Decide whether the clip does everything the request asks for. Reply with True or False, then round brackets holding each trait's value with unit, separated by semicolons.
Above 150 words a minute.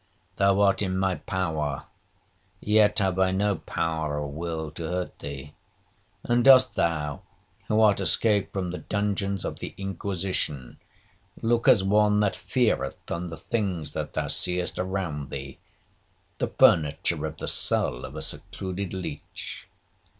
False (145 wpm)